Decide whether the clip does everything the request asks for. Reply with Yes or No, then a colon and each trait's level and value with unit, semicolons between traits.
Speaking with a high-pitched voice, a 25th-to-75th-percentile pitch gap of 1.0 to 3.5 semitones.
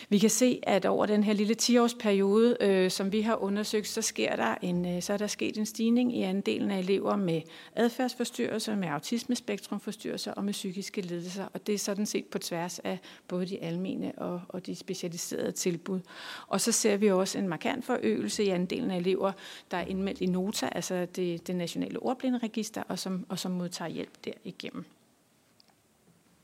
Yes: high, 200 Hz; average, 3.2 semitones